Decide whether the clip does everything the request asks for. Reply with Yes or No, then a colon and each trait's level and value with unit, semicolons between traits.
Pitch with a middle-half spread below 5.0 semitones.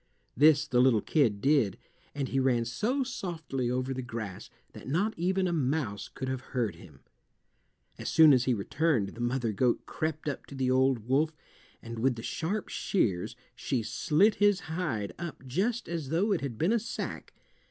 No: average, 5.3 semitones